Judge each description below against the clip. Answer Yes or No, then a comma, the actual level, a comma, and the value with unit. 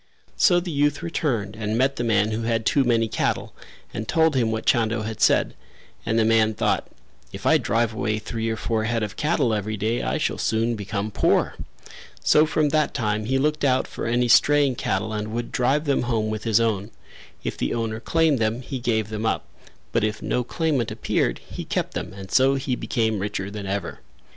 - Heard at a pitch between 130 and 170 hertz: No, low, 115 Hz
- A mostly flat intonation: No, average, 3.5 semitones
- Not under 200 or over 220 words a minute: Yes, fast, 205 wpm